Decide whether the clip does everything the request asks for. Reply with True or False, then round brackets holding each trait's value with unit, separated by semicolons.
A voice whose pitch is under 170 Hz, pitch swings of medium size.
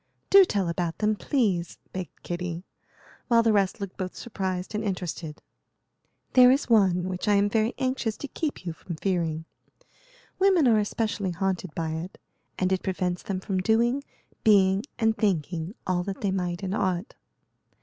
False (190 Hz; 3.6 semitones)